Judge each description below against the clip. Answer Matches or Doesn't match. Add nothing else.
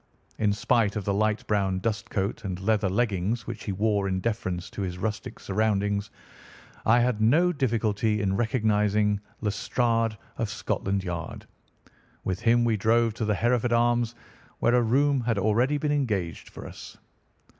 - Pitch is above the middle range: Doesn't match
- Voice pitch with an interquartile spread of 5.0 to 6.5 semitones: Doesn't match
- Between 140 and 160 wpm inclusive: Matches